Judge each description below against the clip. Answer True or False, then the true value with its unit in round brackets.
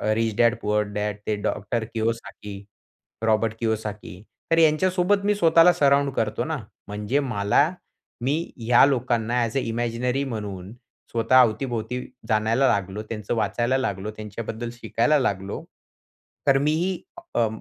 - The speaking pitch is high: False (115 Hz)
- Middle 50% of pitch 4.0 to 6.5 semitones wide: True (4.3 semitones)